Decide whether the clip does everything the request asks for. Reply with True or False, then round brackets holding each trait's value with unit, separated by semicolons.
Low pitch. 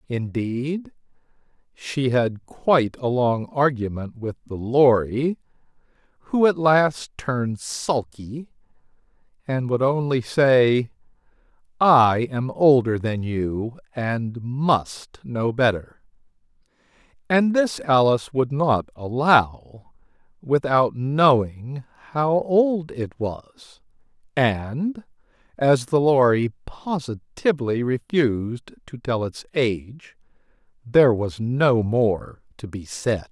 True (130 Hz)